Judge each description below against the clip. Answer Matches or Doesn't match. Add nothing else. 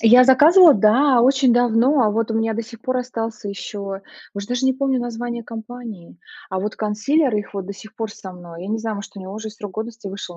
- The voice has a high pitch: Matches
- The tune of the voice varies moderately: Matches